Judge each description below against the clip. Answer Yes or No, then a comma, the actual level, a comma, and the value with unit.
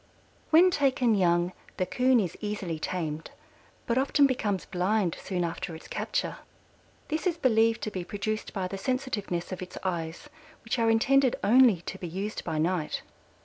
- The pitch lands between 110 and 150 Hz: No, high, 205 Hz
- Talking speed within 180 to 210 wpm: No, average, 165 wpm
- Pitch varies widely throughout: Yes, wide, 5.9 semitones